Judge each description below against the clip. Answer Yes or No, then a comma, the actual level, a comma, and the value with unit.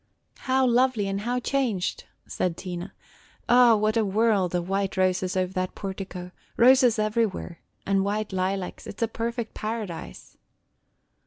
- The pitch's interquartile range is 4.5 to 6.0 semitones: No, average, 3.8 semitones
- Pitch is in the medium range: No, high, 205 Hz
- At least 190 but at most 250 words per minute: No, average, 150 wpm